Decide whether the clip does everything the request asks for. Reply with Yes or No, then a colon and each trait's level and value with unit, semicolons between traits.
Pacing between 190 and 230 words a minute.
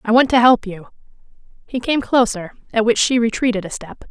Yes: fast, 205 wpm